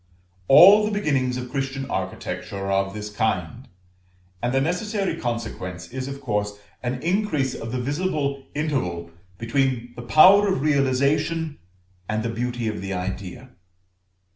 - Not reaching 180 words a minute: Yes, average, 140 wpm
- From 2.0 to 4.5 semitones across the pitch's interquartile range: No, wide, 5.4 semitones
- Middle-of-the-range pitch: No, low, 130 Hz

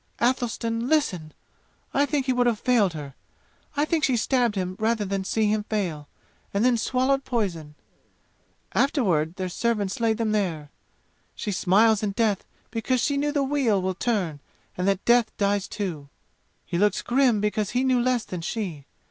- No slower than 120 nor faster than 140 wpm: No, average, 170 wpm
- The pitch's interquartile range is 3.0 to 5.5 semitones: Yes, average, 4.7 semitones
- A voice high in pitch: Yes, high, 215 Hz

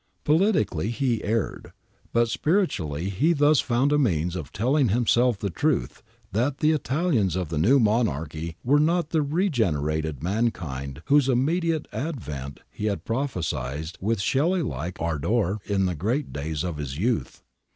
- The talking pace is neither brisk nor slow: Yes, average, 150 wpm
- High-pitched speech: No, low, 110 Hz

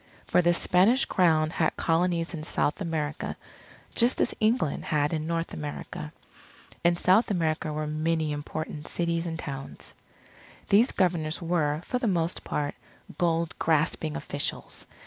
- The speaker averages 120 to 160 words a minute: Yes, average, 140 wpm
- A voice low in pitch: No, medium, 165 Hz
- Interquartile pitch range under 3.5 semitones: Yes, narrow, 2.4 semitones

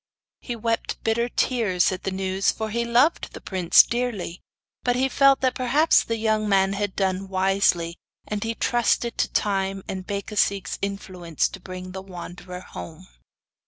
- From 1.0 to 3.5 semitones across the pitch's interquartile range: No, average, 3.9 semitones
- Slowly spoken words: No, average, 160 wpm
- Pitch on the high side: Yes, high, 200 Hz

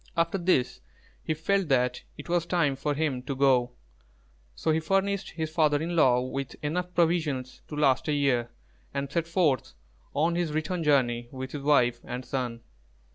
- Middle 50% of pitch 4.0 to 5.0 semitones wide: Yes, average, 4.4 semitones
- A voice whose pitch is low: No, medium, 150 Hz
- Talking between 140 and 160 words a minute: No, average, 175 wpm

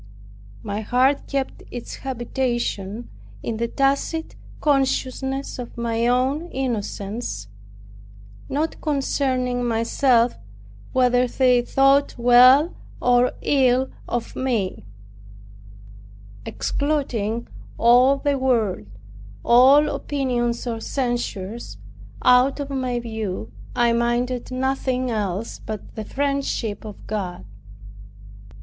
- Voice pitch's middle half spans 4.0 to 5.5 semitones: No, narrow, 2.6 semitones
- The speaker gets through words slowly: Yes, slow, 95 wpm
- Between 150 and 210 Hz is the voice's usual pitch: No, high, 245 Hz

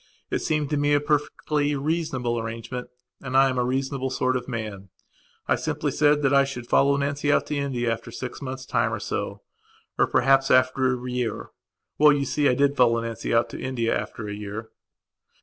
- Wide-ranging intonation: No, average, 2.9 semitones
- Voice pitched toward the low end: Yes, low, 130 Hz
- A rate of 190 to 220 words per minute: Yes, average, 200 wpm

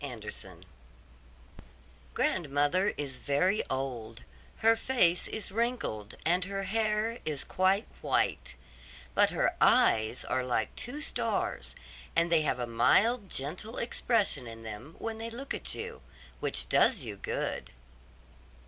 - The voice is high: No, medium, 170 Hz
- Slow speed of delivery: Yes, slow, 130 wpm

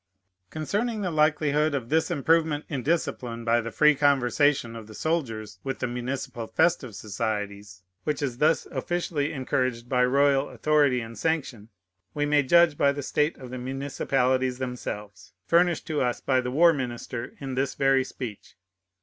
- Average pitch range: Yes, average, 3.9 semitones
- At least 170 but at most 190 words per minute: No, average, 160 wpm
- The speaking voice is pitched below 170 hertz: Yes, low, 135 Hz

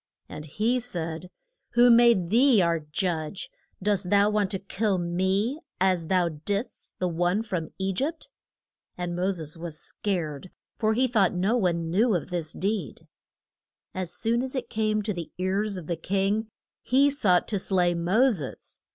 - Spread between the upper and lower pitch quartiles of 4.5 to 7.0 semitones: No, average, 4.0 semitones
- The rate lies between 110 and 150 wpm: No, average, 170 wpm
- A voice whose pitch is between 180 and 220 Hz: Yes, high, 190 Hz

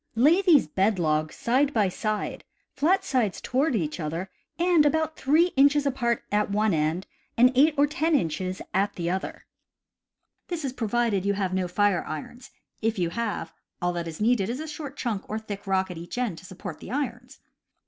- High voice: Yes, high, 220 Hz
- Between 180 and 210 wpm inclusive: Yes, average, 190 wpm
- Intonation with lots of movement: Yes, wide, 6.8 semitones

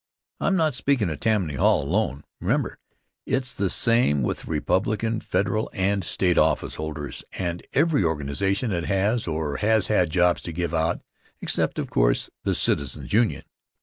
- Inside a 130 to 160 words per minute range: Yes, average, 155 wpm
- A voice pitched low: Yes, very low, 95 Hz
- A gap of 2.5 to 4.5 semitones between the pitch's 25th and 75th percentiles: No, wide, 5.6 semitones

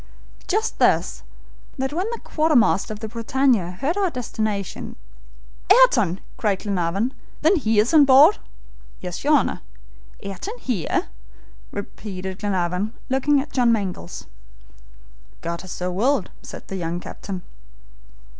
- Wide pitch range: Yes, wide, 6.8 semitones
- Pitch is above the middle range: Yes, high, 215 Hz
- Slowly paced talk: Yes, slow, 130 wpm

